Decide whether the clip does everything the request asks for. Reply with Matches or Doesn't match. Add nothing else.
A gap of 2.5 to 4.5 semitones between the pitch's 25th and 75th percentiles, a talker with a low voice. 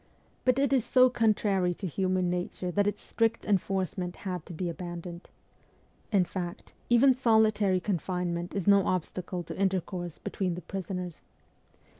Doesn't match